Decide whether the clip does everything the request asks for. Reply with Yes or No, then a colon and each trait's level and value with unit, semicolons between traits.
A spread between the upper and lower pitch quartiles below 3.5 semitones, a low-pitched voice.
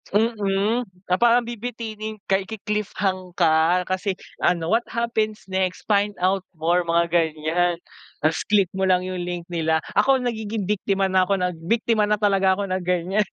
No: average, 3.0 semitones; high, 195 Hz